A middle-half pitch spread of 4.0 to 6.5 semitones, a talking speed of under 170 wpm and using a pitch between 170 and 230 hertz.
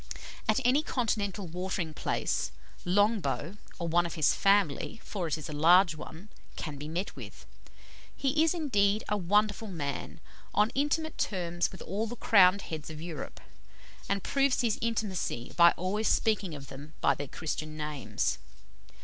Yes: average, 5.1 semitones; average, 160 wpm; medium, 185 Hz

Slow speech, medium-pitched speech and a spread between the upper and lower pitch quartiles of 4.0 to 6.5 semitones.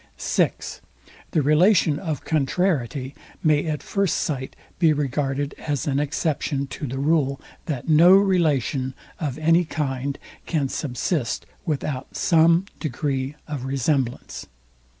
No: slow, 120 wpm; medium, 145 Hz; average, 3.0 semitones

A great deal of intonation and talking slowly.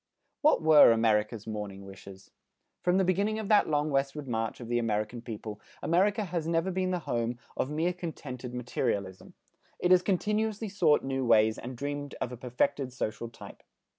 No: wide, 7.6 semitones; average, 170 wpm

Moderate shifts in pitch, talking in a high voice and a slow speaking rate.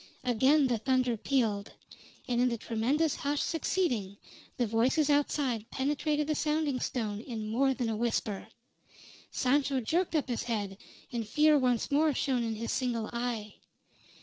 No: average, 4.2 semitones; very high, 250 Hz; average, 150 wpm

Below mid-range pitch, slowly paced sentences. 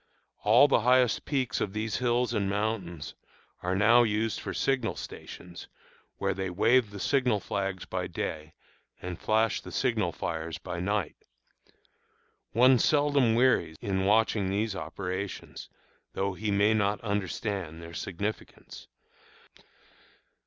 Yes: low, 105 Hz; slow, 125 wpm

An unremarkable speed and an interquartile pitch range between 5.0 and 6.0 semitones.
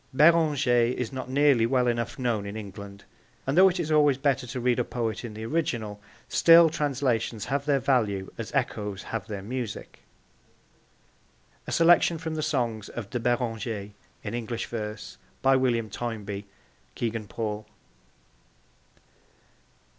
No: average, 145 wpm; average, 4.2 semitones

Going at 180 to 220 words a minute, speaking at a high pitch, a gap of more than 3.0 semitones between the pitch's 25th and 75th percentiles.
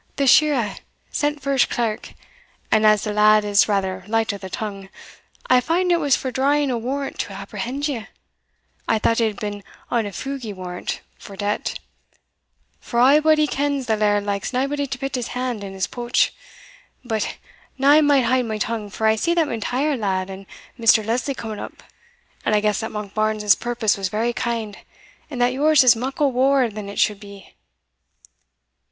Yes: average, 185 wpm; high, 230 Hz; average, 4.4 semitones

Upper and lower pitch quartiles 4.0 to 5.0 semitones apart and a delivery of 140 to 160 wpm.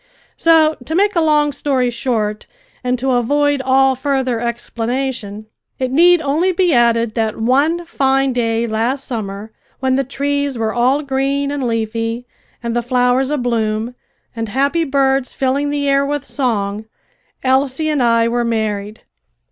No: average, 3.4 semitones; average, 150 wpm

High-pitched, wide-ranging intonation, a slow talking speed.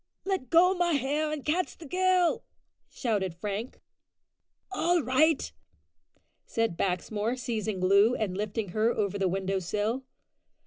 Yes: high, 230 Hz; wide, 7.5 semitones; slow, 130 wpm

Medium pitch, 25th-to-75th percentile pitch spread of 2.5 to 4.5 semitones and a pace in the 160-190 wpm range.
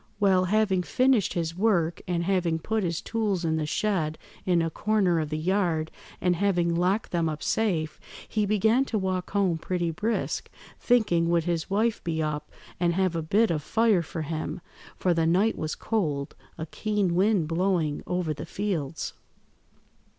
Yes: medium, 175 Hz; average, 4.0 semitones; average, 170 wpm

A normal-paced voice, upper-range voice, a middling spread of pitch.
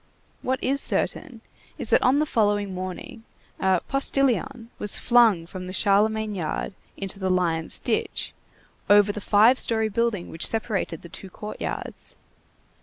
Yes: average, 150 wpm; high, 205 Hz; average, 3.7 semitones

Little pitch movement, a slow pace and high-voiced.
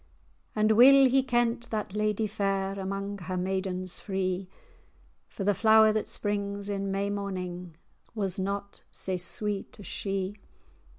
No: narrow, 1.8 semitones; average, 145 wpm; high, 200 Hz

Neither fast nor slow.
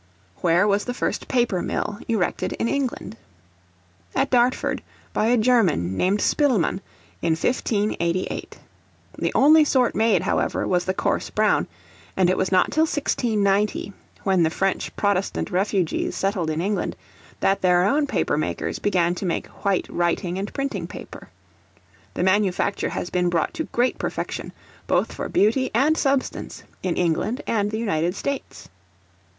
Yes: average, 150 wpm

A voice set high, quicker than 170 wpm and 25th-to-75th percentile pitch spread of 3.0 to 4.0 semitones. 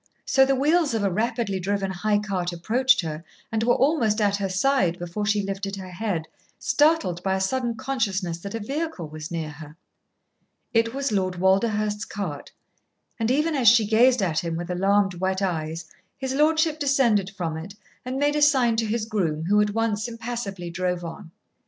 No: high, 205 Hz; average, 185 wpm; average, 5.1 semitones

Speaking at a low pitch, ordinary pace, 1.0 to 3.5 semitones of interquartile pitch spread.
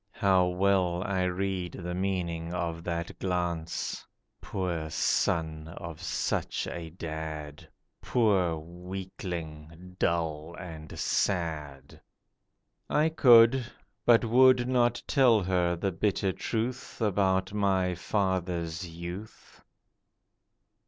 No: very low, 90 Hz; slow, 95 wpm; average, 2.9 semitones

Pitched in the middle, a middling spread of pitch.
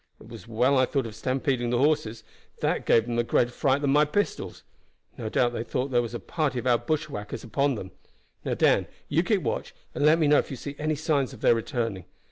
No: low, 130 Hz; average, 3.7 semitones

